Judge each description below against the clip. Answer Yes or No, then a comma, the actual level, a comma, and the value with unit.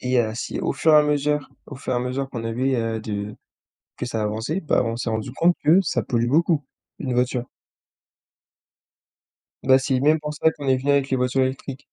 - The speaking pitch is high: No, low, 130 Hz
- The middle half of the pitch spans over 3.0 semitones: Yes, average, 3.5 semitones